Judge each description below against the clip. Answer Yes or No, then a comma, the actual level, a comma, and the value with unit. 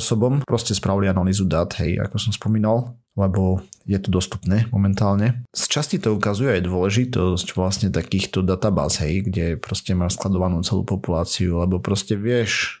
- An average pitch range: Yes, average, 3.0 semitones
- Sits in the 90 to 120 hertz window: Yes, low, 100 Hz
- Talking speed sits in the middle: Yes, average, 155 wpm